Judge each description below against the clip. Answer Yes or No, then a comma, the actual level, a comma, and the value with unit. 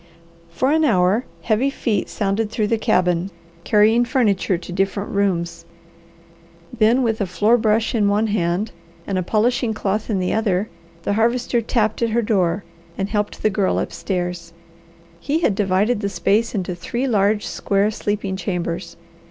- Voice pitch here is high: Yes, high, 210 Hz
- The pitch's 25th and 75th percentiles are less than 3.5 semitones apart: Yes, average, 3.0 semitones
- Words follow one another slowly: No, average, 160 wpm